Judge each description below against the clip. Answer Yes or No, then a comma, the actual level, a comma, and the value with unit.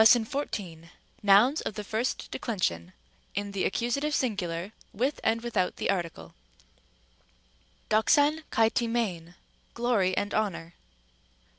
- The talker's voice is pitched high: Yes, high, 215 Hz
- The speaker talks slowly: Yes, slow, 115 wpm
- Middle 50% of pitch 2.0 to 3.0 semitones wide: No, average, 4.6 semitones